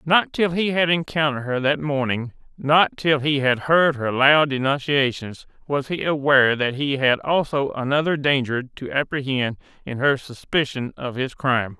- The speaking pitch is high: No, medium, 140 Hz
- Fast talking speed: No, average, 160 wpm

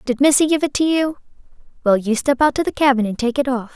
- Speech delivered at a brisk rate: Yes, fast, 270 wpm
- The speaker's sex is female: Yes, female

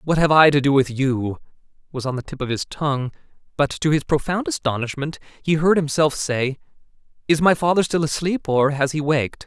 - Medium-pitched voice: Yes, medium, 145 Hz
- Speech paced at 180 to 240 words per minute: Yes, fast, 205 wpm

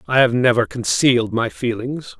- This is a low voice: Yes, low, 120 Hz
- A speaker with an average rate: Yes, average, 165 wpm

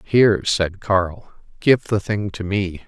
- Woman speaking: No, male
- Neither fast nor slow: Yes, average, 165 wpm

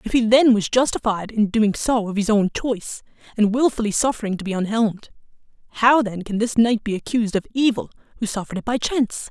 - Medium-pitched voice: No, high, 220 Hz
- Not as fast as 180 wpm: No, fast, 205 wpm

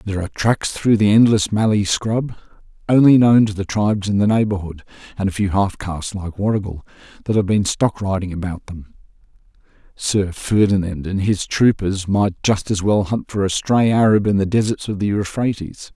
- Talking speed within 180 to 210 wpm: Yes, average, 190 wpm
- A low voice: Yes, low, 100 Hz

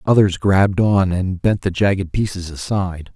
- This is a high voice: No, very low, 95 Hz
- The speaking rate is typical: Yes, average, 170 wpm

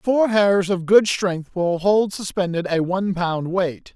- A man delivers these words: Yes, male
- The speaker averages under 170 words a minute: No, average, 180 wpm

